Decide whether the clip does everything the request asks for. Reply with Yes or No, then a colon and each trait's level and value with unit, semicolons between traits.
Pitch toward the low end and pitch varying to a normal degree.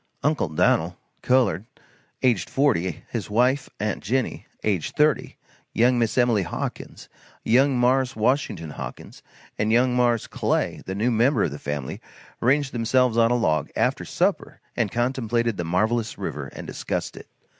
Yes: low, 115 Hz; average, 3.7 semitones